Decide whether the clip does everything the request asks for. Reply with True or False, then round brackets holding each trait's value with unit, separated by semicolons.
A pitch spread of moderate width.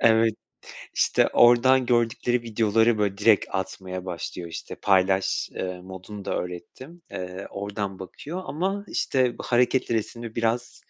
True (4.3 semitones)